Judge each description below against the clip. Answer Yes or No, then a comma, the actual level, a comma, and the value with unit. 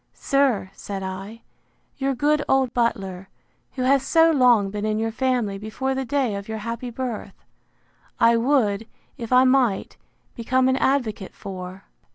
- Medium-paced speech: Yes, average, 155 wpm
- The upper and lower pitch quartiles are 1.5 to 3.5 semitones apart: No, average, 4.3 semitones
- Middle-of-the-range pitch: No, high, 235 Hz